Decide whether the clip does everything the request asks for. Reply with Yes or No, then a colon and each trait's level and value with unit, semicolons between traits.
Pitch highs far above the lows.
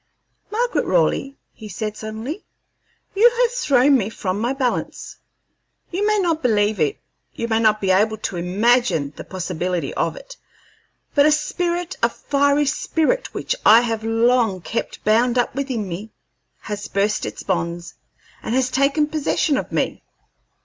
Yes: wide, 6.0 semitones